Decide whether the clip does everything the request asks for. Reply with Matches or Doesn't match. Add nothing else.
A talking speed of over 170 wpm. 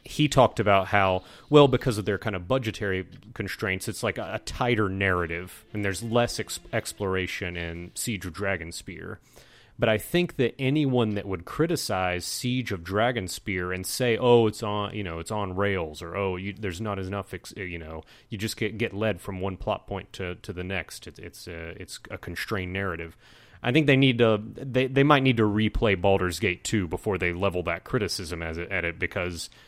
Matches